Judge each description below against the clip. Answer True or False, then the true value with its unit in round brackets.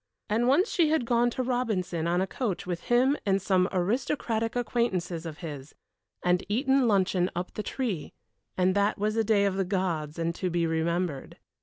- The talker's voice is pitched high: True (195 Hz)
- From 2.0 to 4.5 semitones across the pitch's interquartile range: False (5.2 semitones)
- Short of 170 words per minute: False (185 wpm)